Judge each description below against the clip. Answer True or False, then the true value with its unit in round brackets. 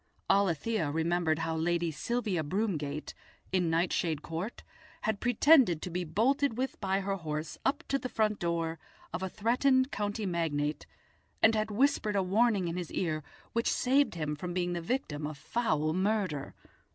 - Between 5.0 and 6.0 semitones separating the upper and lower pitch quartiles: True (5.3 semitones)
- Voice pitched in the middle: True (180 Hz)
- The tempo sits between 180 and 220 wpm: False (165 wpm)